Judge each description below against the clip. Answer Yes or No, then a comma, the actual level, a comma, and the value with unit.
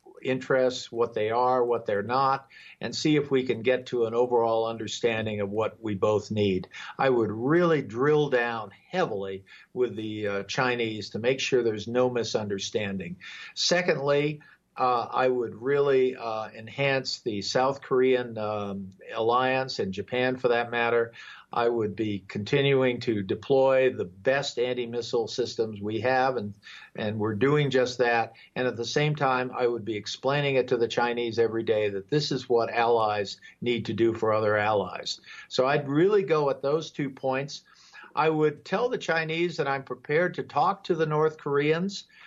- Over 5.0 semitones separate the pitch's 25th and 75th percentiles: No, average, 3.6 semitones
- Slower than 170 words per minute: No, average, 175 wpm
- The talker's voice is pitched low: Yes, low, 125 Hz